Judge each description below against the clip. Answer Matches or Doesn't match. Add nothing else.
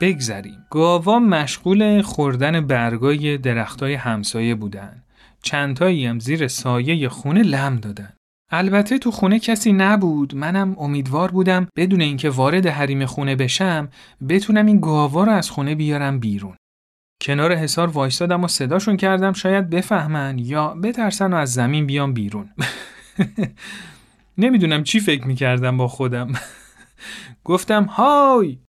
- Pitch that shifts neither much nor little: Doesn't match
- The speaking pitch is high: Doesn't match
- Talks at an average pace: Matches